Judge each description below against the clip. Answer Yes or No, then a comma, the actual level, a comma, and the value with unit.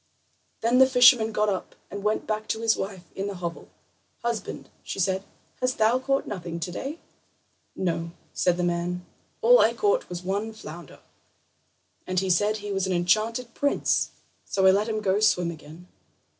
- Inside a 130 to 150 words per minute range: No, average, 170 wpm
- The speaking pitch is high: Yes, high, 200 Hz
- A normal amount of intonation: Yes, average, 3.9 semitones